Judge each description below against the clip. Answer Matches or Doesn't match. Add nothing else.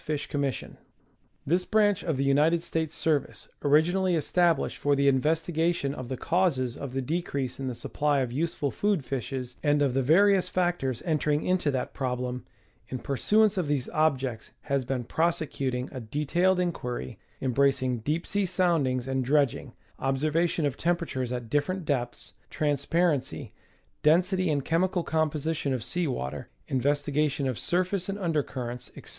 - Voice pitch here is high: Doesn't match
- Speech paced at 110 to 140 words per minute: Doesn't match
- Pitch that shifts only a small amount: Doesn't match